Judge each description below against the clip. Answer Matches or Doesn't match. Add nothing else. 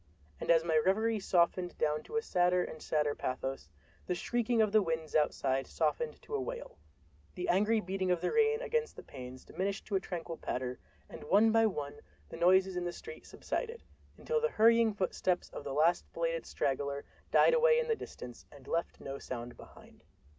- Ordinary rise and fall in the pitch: Doesn't match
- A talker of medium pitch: Matches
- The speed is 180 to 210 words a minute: Matches